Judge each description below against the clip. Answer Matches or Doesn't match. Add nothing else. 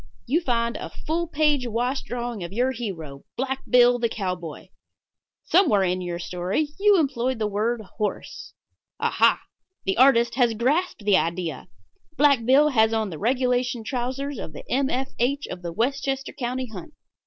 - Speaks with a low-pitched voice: Doesn't match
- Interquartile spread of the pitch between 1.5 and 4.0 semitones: Doesn't match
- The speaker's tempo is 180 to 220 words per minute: Doesn't match